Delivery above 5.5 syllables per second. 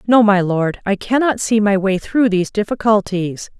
No: 4.9 syllables/s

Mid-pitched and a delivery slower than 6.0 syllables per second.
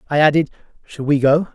No: medium, 150 Hz; 6.3 syllables/s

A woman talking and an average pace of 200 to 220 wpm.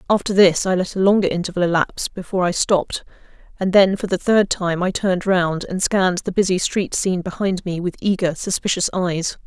Yes: female; fast, 205 wpm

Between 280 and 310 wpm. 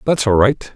No: fast, 240 wpm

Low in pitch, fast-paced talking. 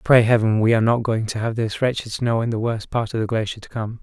Yes: low, 115 Hz; fast, 300 wpm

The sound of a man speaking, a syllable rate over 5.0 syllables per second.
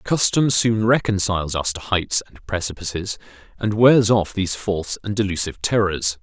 Yes: male; 5.2 syllables/s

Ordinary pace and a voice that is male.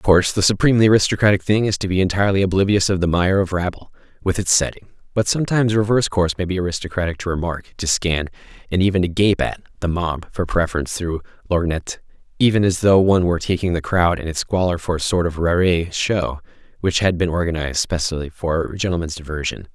No: fast, 210 wpm; male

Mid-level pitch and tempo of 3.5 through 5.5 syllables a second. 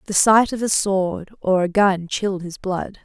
No: high, 195 Hz; 4.4 syllables/s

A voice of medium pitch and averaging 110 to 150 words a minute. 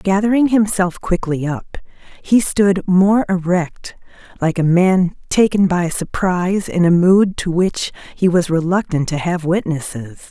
Yes: medium, 180 Hz; average, 145 wpm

